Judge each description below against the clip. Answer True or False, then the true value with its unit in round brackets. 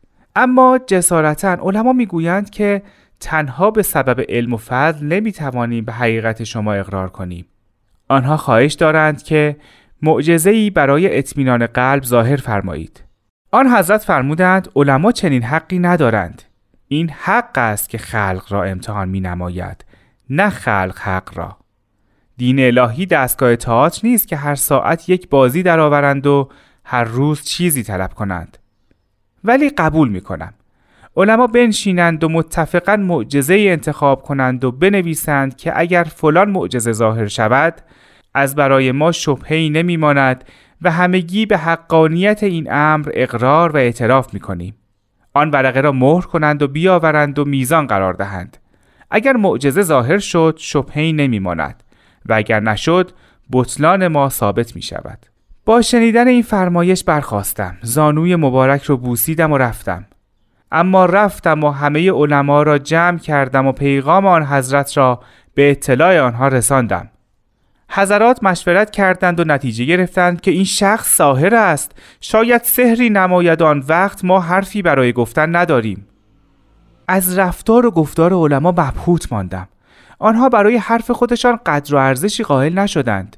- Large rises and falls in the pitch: True (7.1 semitones)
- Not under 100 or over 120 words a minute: False (135 wpm)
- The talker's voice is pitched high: False (145 Hz)